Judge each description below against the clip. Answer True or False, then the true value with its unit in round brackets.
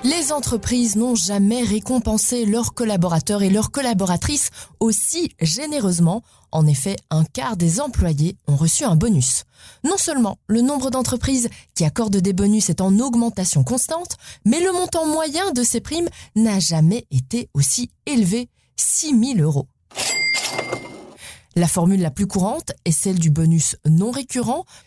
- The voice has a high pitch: True (215 Hz)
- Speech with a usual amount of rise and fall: False (6.5 semitones)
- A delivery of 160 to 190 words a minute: False (145 wpm)